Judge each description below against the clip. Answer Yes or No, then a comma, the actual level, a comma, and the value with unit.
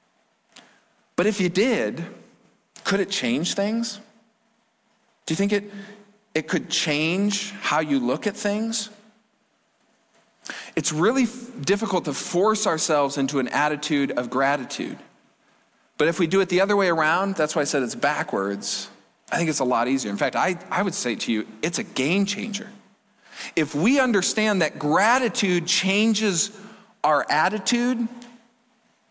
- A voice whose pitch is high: Yes, high, 200 Hz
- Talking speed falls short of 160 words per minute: Yes, average, 150 wpm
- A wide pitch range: Yes, wide, 5.8 semitones